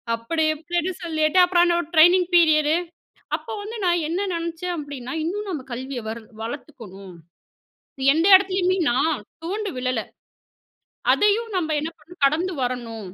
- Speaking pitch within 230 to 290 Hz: No, very high, 320 Hz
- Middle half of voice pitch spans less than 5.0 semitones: No, average, 5.3 semitones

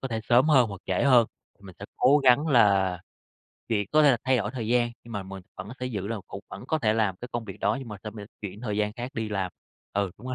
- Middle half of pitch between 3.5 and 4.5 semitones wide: Yes, average, 3.8 semitones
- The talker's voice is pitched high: No, low, 110 Hz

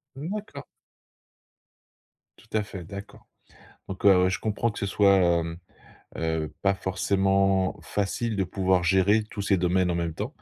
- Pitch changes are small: Yes, narrow, 2.1 semitones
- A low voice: Yes, very low, 95 Hz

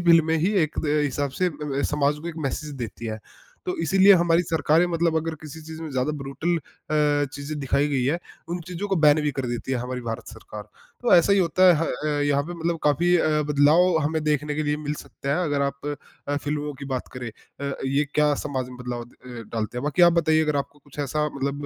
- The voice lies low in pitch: No, medium, 150 Hz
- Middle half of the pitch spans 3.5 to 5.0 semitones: No, average, 2.8 semitones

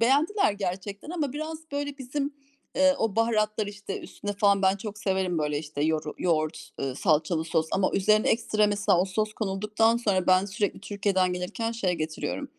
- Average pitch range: Yes, average, 3.7 semitones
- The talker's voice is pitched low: No, high, 200 Hz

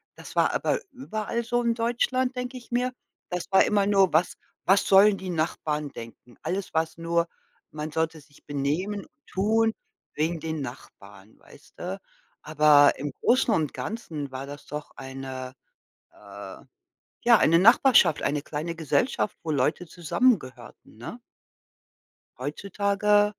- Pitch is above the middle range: No, medium, 170 Hz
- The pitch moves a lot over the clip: Yes, wide, 6.3 semitones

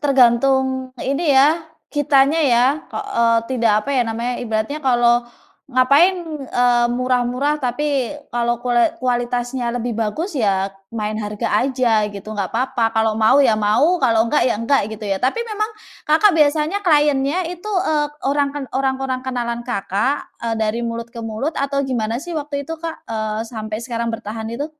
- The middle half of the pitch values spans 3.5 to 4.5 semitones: Yes, average, 3.8 semitones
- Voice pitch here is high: Yes, very high, 250 Hz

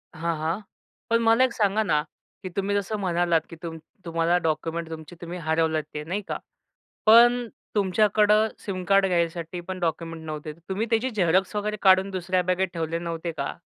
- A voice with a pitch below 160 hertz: No, medium, 180 Hz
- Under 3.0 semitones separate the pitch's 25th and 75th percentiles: No, average, 3.6 semitones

